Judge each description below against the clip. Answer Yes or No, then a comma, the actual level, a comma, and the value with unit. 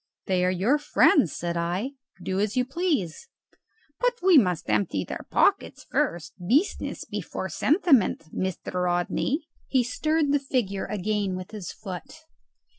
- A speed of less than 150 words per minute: Yes, average, 140 wpm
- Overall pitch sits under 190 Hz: No, high, 210 Hz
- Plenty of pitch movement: Yes, wide, 8.0 semitones